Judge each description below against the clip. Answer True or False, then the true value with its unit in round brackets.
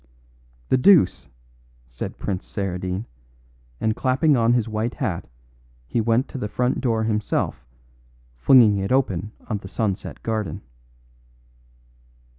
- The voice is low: True (110 Hz)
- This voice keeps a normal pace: False (120 wpm)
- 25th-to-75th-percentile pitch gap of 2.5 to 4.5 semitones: True (4.1 semitones)